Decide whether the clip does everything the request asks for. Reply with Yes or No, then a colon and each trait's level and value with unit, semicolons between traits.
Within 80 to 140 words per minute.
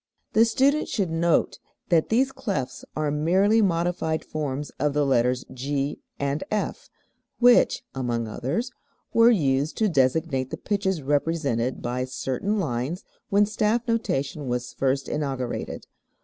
Yes: slow, 135 wpm